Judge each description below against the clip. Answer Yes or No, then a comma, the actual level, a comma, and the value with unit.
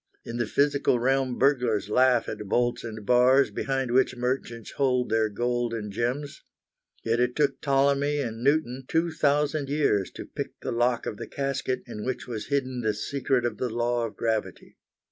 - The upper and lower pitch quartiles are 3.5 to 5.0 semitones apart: No, average, 2.9 semitones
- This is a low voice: Yes, low, 125 Hz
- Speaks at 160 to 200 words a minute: Yes, average, 175 wpm